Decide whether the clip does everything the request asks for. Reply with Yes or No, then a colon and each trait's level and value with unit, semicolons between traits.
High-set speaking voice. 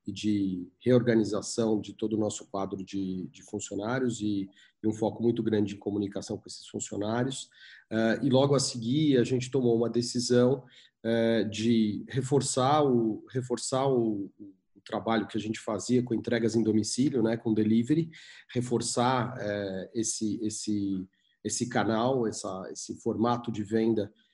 No: low, 110 Hz